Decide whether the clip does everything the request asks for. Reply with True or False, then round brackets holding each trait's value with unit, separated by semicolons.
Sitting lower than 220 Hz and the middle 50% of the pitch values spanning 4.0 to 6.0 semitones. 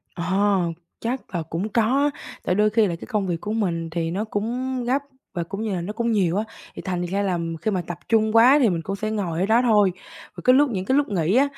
True (205 Hz; 4.3 semitones)